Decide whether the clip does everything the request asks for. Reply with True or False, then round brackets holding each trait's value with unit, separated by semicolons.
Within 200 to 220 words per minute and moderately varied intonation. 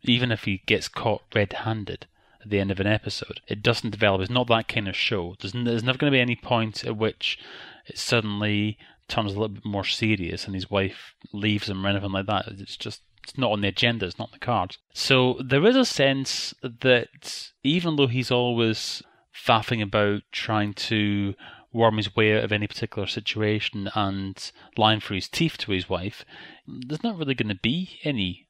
True (205 wpm; 3.3 semitones)